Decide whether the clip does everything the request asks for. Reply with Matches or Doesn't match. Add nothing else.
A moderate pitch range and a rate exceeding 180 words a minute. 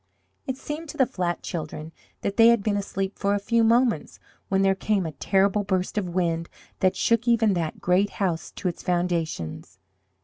Matches